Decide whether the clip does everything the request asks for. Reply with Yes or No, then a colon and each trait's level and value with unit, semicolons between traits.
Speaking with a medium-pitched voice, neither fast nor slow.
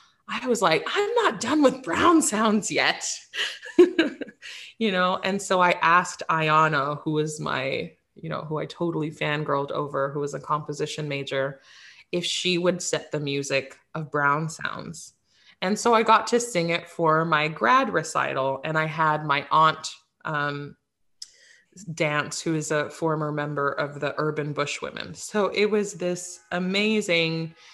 Yes: medium, 160 Hz; average, 160 wpm